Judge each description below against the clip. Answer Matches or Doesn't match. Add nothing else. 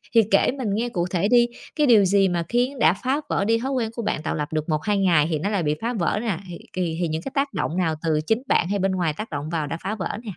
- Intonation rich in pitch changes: Matches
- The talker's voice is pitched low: Doesn't match